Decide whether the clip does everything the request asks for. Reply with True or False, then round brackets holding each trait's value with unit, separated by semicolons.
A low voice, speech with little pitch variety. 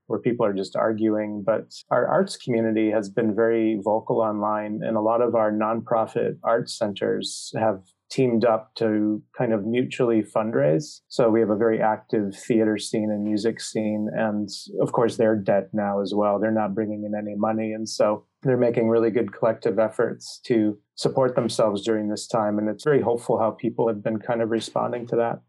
True (110 Hz; 1.2 semitones)